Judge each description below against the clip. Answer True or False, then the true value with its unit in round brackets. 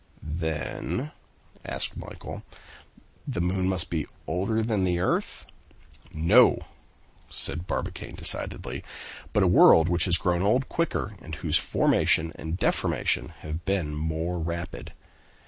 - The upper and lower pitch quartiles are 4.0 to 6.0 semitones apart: False (2.9 semitones)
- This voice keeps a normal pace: False (125 wpm)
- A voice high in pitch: False (85 Hz)